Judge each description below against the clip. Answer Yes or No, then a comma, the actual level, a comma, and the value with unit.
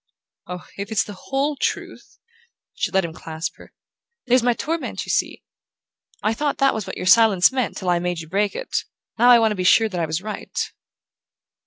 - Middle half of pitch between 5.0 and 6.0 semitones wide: Yes, average, 5.3 semitones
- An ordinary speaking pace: No, fast, 210 wpm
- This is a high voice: Yes, high, 210 Hz